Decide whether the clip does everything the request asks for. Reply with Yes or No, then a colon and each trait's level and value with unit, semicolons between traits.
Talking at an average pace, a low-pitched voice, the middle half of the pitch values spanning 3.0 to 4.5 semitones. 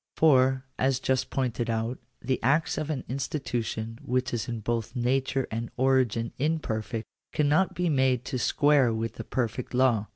No: average, 165 wpm; low, 130 Hz; narrow, 2.6 semitones